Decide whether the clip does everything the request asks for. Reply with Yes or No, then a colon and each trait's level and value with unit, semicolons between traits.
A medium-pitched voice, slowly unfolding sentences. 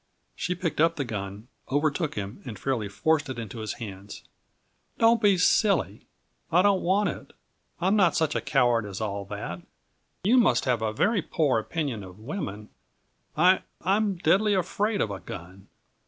No: medium, 145 Hz; average, 170 wpm